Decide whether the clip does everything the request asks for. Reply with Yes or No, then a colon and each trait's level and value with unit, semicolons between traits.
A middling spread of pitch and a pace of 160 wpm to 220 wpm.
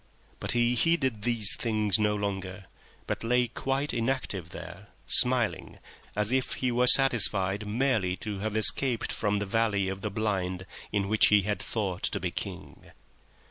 Yes: average, 3.4 semitones; average, 165 wpm